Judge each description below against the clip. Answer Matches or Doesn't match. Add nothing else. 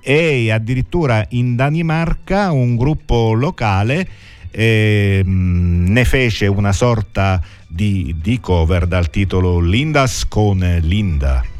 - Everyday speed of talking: Doesn't match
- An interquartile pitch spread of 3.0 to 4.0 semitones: Doesn't match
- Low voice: Matches